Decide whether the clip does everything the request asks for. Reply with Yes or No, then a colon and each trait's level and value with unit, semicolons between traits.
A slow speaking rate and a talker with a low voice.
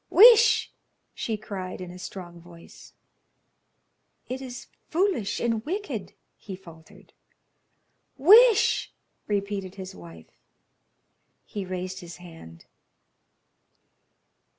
No: slow, 90 wpm; high, 195 Hz